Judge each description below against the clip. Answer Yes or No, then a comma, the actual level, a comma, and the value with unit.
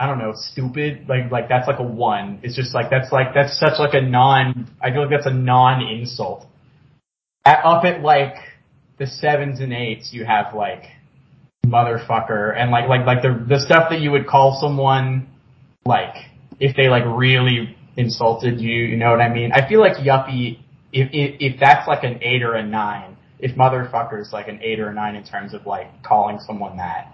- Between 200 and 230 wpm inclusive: Yes, fast, 205 wpm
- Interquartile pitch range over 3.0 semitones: No, average, 2.7 semitones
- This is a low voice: Yes, low, 130 Hz